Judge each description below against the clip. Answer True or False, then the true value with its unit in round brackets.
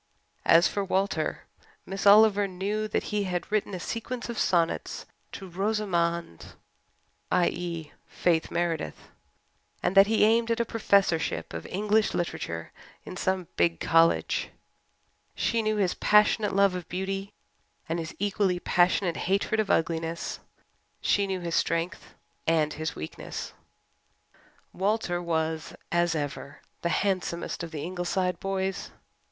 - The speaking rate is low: True (130 wpm)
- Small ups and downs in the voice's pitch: False (3.3 semitones)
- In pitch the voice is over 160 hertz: True (185 Hz)